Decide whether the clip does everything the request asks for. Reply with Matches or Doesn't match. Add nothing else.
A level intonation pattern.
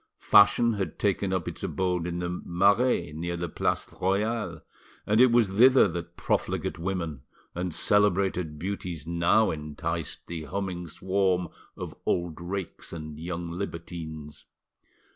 Doesn't match